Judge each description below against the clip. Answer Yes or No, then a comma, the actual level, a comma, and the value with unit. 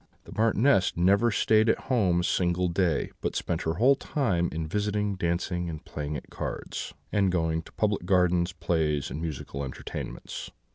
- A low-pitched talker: Yes, very low, 90 Hz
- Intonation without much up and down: No, average, 4.0 semitones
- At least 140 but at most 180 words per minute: Yes, average, 170 wpm